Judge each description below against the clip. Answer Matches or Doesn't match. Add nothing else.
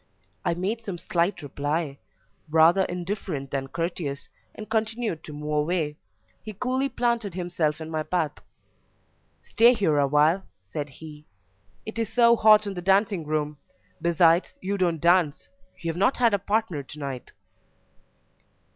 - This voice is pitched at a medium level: Matches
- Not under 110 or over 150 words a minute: Matches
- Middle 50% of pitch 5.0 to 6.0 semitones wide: Matches